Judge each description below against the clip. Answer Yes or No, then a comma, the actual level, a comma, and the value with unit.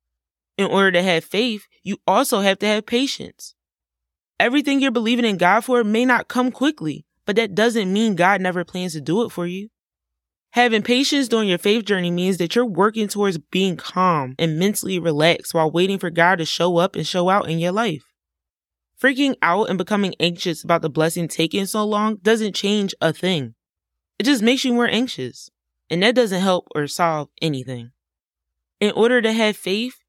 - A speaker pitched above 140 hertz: Yes, high, 190 Hz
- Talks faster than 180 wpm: Yes, average, 190 wpm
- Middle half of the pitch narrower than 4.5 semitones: No, average, 5.3 semitones